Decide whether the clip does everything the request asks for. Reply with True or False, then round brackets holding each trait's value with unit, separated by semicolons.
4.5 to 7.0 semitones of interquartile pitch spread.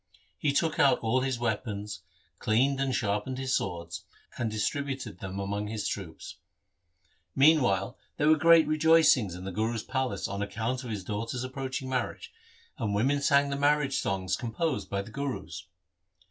True (5.3 semitones)